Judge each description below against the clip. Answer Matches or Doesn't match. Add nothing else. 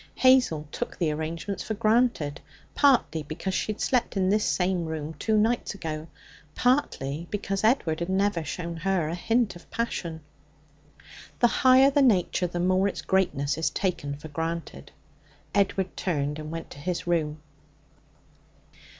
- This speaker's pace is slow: Doesn't match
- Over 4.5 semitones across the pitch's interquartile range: Matches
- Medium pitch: Matches